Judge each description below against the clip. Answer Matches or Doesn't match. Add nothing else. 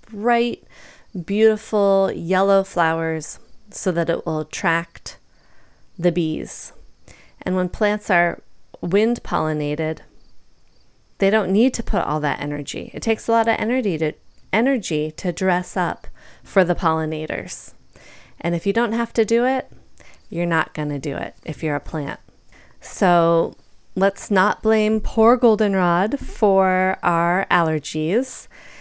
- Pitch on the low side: Doesn't match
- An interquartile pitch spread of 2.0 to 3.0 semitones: Doesn't match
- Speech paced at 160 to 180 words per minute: Doesn't match